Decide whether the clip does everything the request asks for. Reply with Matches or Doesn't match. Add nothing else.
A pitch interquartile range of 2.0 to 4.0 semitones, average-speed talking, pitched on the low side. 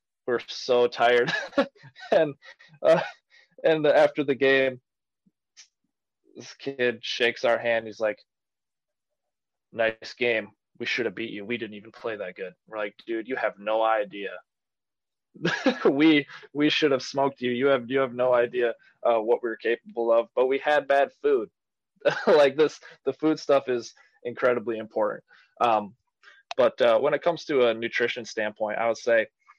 Matches